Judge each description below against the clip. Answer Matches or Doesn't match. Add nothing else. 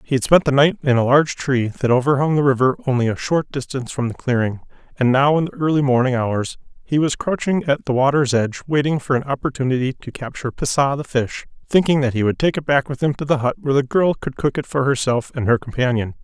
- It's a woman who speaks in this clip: Doesn't match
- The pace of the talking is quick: Matches